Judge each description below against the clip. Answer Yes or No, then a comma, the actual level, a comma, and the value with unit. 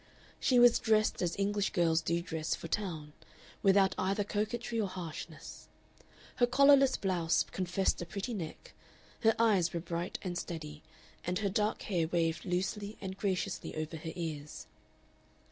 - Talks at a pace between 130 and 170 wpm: Yes, average, 150 wpm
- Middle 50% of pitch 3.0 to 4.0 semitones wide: Yes, average, 3.7 semitones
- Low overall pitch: No, medium, 185 Hz